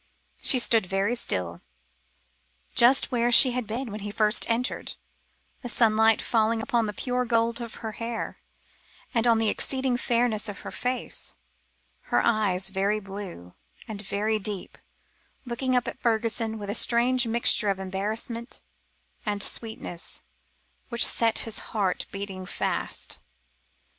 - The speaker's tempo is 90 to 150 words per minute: Yes, average, 140 wpm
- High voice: Yes, high, 225 Hz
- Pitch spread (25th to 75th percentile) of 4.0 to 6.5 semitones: No, narrow, 2.6 semitones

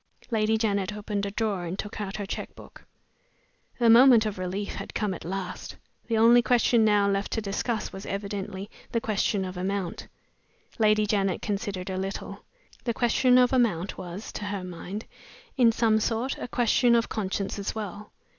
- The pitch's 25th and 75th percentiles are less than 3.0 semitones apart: Yes, narrow, 2.6 semitones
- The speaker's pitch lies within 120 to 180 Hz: No, high, 210 Hz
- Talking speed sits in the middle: Yes, average, 175 wpm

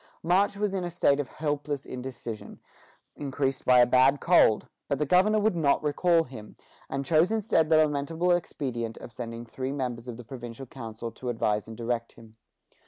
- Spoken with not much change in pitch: No, average, 5.3 semitones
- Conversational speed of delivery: Yes, average, 180 wpm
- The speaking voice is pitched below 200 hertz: Yes, low, 135 Hz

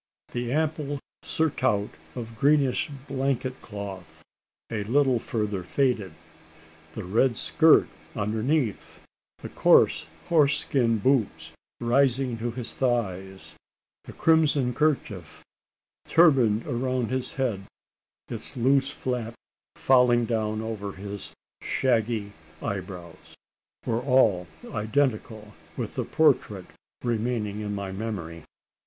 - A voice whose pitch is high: No, low, 115 Hz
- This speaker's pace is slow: Yes, slow, 105 wpm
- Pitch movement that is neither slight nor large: Yes, average, 4.2 semitones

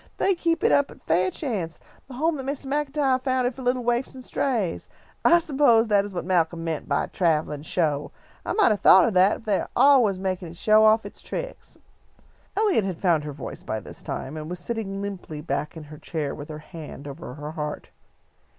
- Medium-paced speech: No, fast, 215 wpm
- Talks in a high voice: Yes, high, 195 Hz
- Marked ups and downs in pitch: Yes, wide, 8.2 semitones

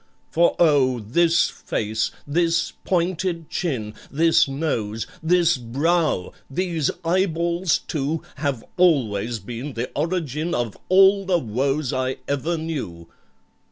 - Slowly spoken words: Yes, slow, 100 wpm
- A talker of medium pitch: Yes, medium, 155 Hz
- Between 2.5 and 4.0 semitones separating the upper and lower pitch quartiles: No, wide, 5.4 semitones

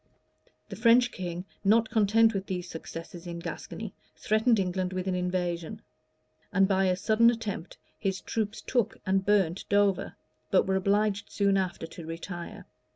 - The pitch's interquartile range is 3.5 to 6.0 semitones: No, average, 2.8 semitones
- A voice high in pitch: Yes, high, 195 Hz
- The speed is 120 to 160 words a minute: Yes, average, 155 wpm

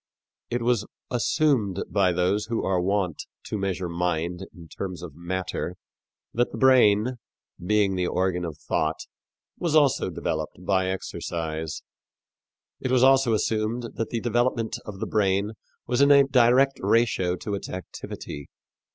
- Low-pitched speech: Yes, low, 100 Hz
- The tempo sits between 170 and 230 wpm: No, average, 145 wpm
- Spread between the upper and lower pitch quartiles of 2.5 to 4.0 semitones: No, average, 5.1 semitones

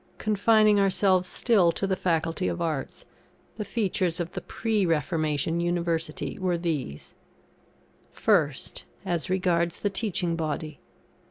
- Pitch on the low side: No, medium, 175 Hz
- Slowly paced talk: Yes, slow, 120 wpm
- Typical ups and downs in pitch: Yes, average, 3.0 semitones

